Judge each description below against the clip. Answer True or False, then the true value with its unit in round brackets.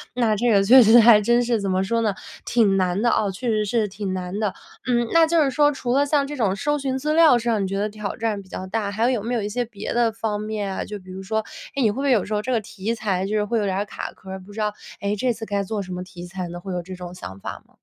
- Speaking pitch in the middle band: False (215 Hz)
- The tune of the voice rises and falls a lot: False (3.6 semitones)